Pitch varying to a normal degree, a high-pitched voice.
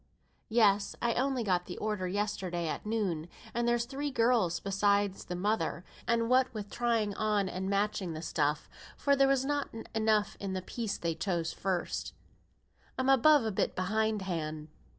Yes: average, 4.3 semitones; high, 205 Hz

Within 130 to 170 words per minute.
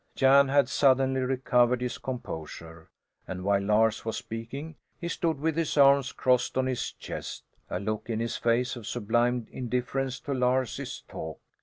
Yes: average, 160 wpm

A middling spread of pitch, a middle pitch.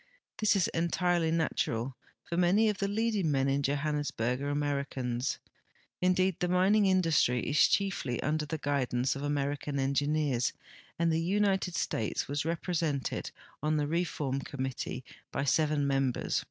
Yes: average, 4.3 semitones; medium, 150 Hz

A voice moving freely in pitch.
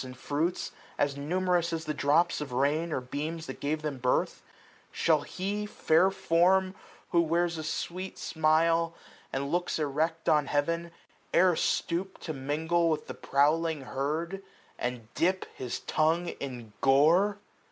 No: average, 3.1 semitones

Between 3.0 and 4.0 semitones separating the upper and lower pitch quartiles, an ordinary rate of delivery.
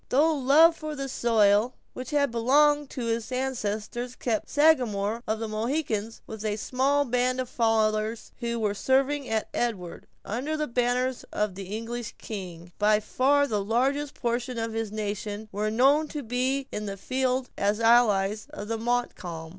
Yes: average, 3.5 semitones; average, 165 wpm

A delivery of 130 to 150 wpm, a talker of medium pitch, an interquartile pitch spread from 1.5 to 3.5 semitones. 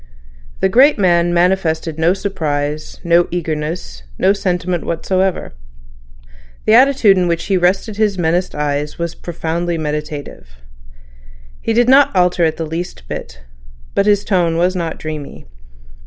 Yes: average, 140 wpm; medium, 175 Hz; average, 3.2 semitones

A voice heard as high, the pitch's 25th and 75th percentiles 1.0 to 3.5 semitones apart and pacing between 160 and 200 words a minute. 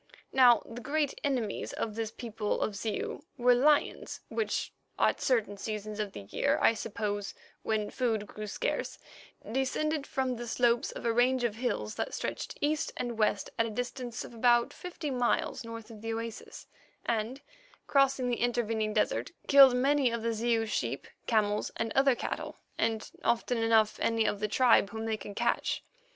Yes: high, 235 Hz; average, 2.8 semitones; average, 170 wpm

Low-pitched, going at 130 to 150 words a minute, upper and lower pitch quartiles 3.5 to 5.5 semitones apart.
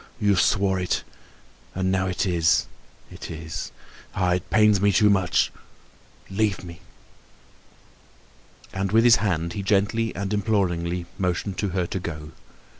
No: very low, 95 Hz; slow, 135 wpm; narrow, 2.6 semitones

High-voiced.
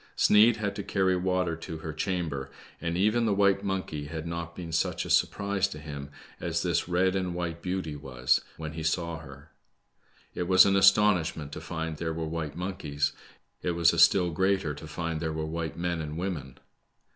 No: very low, 85 Hz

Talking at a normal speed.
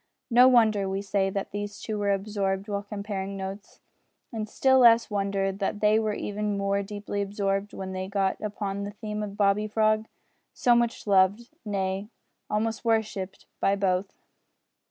Yes: average, 160 wpm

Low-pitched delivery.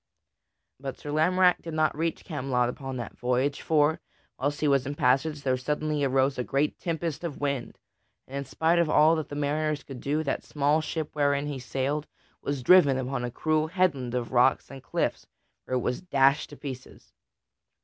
No: medium, 145 Hz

